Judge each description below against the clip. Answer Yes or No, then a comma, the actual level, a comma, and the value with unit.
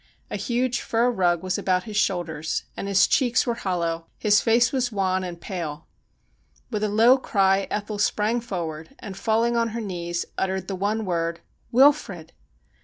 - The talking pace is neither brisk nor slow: Yes, average, 175 wpm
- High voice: Yes, high, 200 Hz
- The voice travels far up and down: No, average, 4.6 semitones